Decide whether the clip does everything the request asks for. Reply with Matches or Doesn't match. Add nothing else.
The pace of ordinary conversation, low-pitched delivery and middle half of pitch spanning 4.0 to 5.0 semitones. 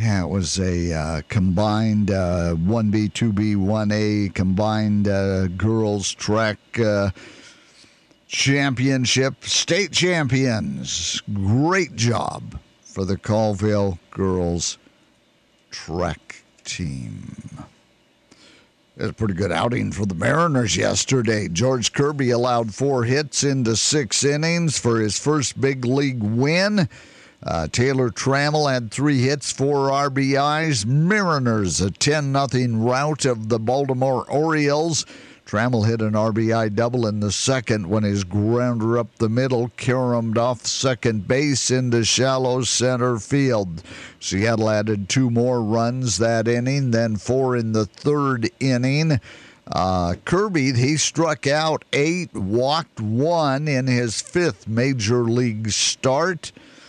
Doesn't match